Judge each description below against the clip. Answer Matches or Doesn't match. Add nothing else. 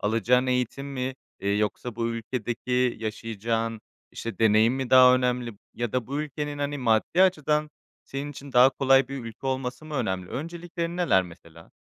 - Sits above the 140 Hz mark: Doesn't match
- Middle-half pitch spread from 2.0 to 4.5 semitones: Matches